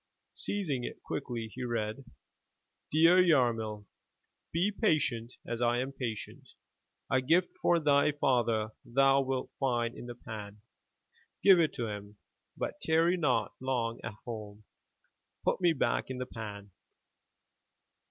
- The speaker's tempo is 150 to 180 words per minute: No, slow, 135 wpm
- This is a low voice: Yes, low, 125 Hz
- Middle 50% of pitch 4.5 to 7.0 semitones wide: Yes, average, 4.8 semitones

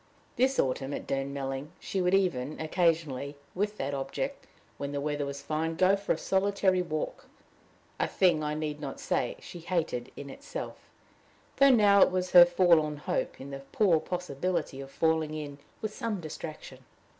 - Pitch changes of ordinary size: Yes, average, 4.7 semitones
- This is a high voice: No, medium, 155 Hz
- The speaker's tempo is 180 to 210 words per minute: No, average, 170 wpm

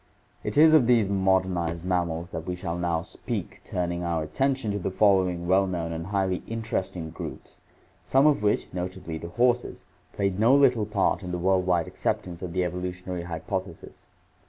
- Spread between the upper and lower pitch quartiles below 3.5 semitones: Yes, average, 2.8 semitones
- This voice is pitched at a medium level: No, very low, 90 Hz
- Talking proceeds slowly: No, average, 175 wpm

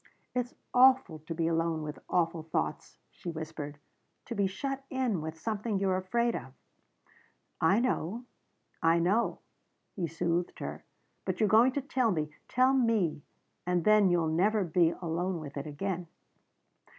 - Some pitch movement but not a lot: No, wide, 5.7 semitones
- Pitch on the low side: No, medium, 180 Hz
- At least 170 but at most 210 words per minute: No, average, 150 wpm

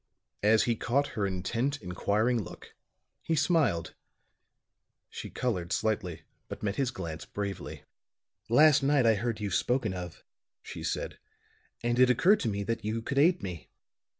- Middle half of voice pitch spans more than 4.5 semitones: Yes, average, 5.0 semitones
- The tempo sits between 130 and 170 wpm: Yes, average, 150 wpm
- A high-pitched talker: No, low, 115 Hz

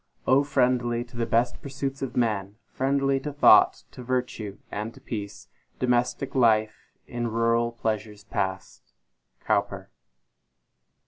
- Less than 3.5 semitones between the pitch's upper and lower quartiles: Yes, average, 2.9 semitones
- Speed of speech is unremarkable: No, slow, 120 wpm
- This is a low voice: Yes, low, 120 Hz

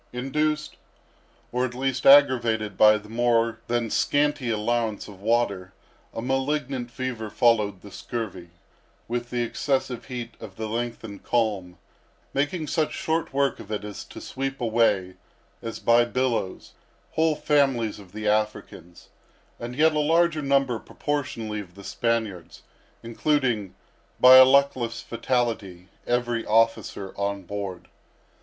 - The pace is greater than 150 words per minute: No, slow, 135 wpm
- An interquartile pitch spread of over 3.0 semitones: Yes, average, 3.9 semitones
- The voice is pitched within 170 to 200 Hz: No, low, 120 Hz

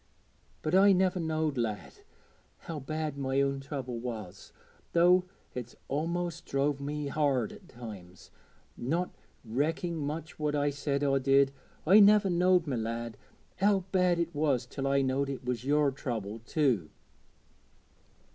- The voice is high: No, medium, 140 Hz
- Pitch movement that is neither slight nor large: Yes, average, 4.6 semitones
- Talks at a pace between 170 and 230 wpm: No, average, 145 wpm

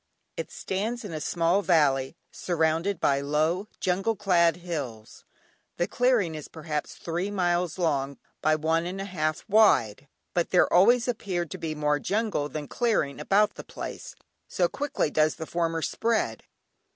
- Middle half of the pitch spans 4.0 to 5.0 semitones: Yes, average, 4.3 semitones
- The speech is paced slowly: No, average, 155 wpm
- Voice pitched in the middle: Yes, medium, 170 Hz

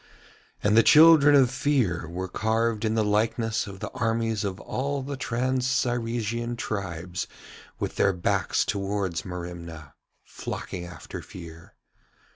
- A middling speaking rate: No, slow, 130 wpm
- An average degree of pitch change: Yes, average, 4.9 semitones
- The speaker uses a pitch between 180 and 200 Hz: No, low, 110 Hz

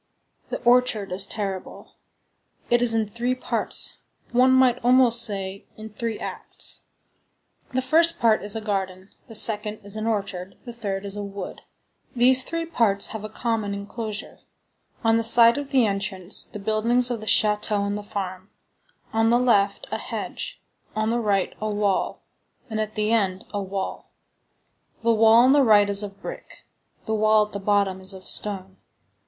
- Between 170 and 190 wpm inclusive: Yes, average, 175 wpm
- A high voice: Yes, high, 215 Hz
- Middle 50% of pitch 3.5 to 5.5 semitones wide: No, average, 2.8 semitones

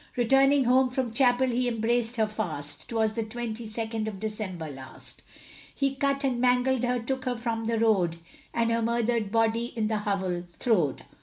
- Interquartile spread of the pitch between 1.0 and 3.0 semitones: Yes, narrow, 2.4 semitones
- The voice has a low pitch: No, high, 230 Hz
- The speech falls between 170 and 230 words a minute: Yes, average, 175 wpm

